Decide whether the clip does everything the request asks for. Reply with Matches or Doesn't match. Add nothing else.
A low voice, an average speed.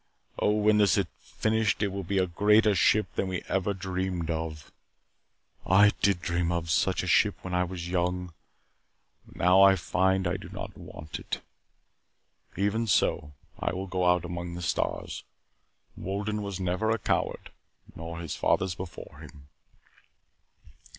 Matches